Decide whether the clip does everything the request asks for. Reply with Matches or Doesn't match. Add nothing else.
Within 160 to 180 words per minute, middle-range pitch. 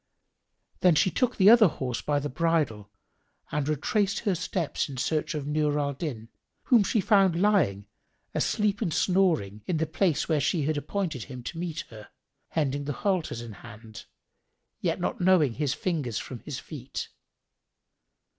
Matches